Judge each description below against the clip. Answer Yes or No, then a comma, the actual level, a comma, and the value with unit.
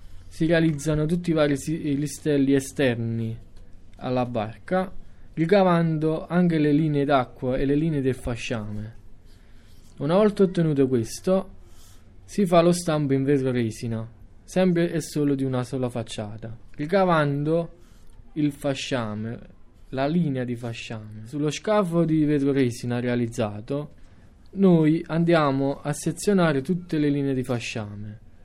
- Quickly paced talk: No, average, 125 wpm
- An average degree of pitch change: No, wide, 5.9 semitones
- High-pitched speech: No, medium, 140 Hz